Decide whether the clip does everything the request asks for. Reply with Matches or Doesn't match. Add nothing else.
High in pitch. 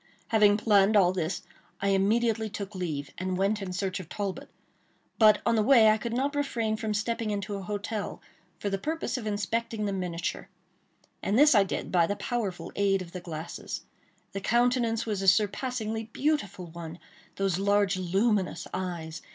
Matches